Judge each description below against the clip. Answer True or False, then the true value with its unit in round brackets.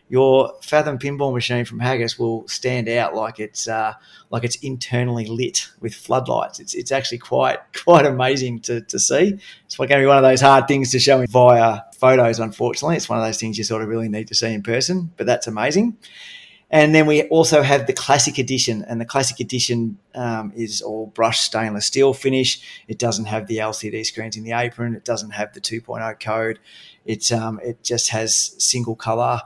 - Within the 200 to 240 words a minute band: True (205 wpm)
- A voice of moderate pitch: False (120 Hz)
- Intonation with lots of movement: False (3.2 semitones)